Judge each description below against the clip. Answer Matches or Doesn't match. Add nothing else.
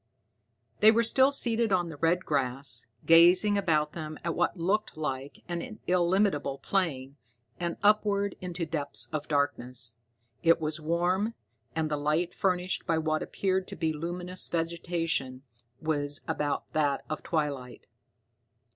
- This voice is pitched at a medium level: Matches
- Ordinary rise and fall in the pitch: Matches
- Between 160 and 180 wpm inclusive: Doesn't match